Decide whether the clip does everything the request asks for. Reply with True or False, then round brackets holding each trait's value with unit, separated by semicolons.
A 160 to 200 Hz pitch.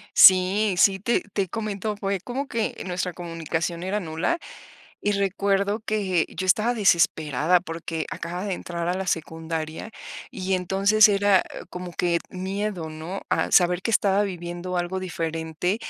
True (185 Hz)